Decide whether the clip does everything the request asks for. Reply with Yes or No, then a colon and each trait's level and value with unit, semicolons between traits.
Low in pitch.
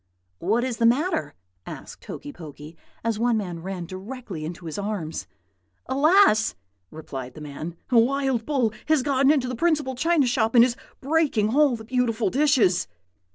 No: high, 235 Hz